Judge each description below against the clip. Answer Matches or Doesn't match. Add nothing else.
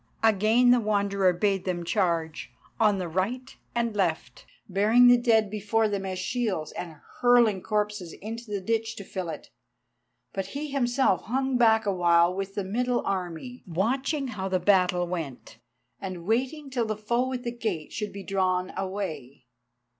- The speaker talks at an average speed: Matches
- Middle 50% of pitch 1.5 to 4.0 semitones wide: Doesn't match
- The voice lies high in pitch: Matches